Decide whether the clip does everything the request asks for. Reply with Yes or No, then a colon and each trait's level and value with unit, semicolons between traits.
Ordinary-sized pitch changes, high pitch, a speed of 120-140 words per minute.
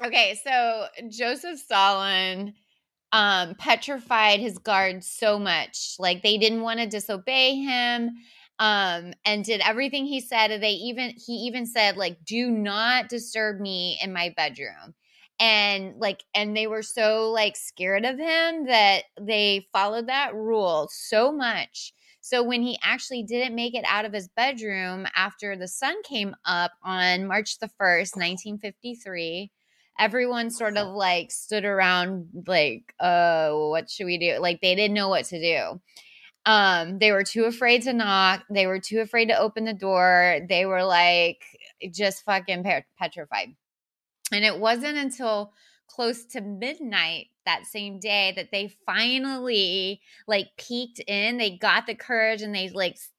No: average, 3.6 semitones; high, 210 Hz; average, 155 wpm